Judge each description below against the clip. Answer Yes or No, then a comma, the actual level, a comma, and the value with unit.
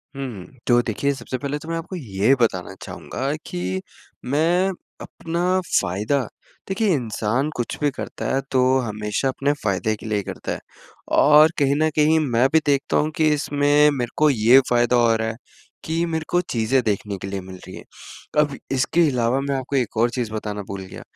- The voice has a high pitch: No, low, 130 Hz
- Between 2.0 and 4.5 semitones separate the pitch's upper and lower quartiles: No, wide, 5.4 semitones